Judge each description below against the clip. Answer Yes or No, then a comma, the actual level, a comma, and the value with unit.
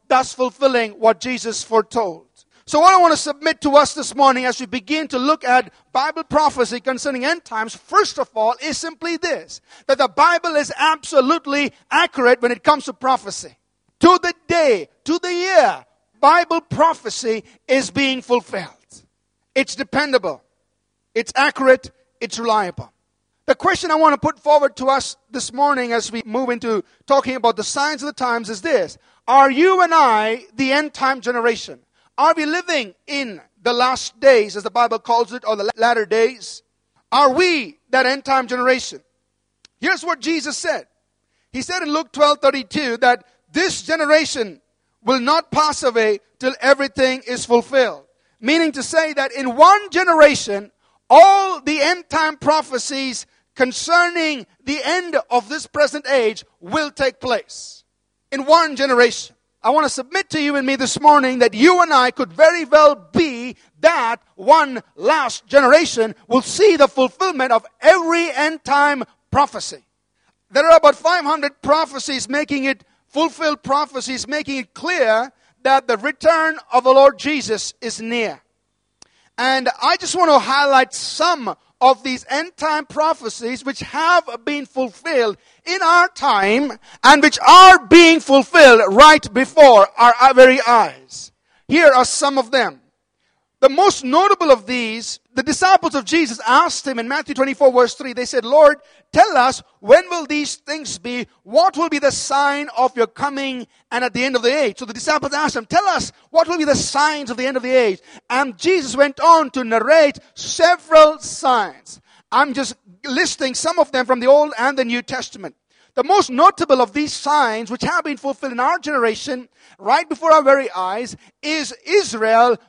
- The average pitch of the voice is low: No, very high, 275 Hz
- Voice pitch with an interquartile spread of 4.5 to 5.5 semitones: No, average, 3.9 semitones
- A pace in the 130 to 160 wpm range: No, average, 170 wpm